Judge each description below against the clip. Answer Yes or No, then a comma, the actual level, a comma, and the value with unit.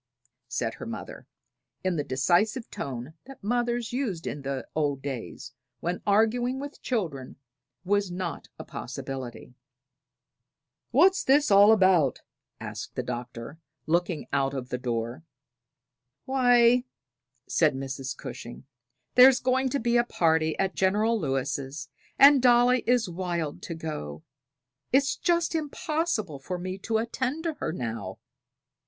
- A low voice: No, medium, 180 Hz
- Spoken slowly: Yes, slow, 130 wpm